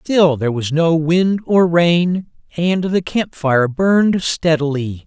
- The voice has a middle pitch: Yes, medium, 165 Hz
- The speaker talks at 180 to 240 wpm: No, average, 140 wpm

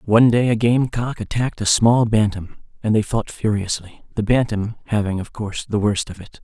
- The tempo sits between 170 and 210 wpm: Yes, fast, 205 wpm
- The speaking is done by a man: Yes, male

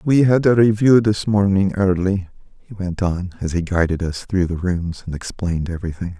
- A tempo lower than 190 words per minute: No, average, 195 wpm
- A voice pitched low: Yes, very low, 95 Hz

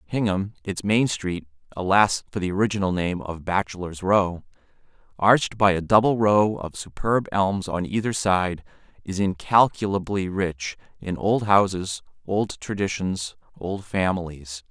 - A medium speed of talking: No, slow, 125 wpm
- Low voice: Yes, very low, 95 Hz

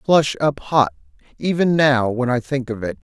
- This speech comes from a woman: No, male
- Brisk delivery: Yes, fast, 210 wpm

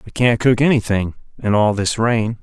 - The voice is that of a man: Yes, male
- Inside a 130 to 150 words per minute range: No, average, 200 wpm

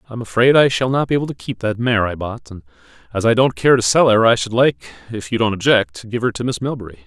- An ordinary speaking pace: No, fast, 280 wpm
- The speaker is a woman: No, male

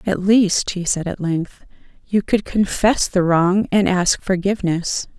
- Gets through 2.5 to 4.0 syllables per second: Yes, 3.9 syllables/s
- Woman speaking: Yes, female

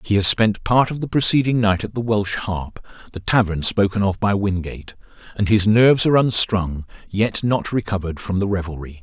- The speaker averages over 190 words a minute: No, average, 185 wpm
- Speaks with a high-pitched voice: No, low, 100 Hz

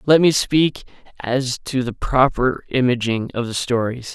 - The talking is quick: No, average, 160 wpm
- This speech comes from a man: Yes, male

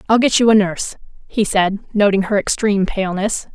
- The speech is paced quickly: No, average, 185 wpm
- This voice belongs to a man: No, female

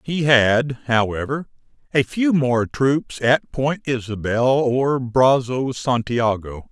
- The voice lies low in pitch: Yes, low, 125 Hz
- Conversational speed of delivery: No, slow, 115 wpm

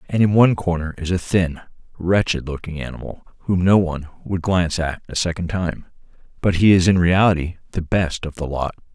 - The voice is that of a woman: No, male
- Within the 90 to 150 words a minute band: No, average, 195 wpm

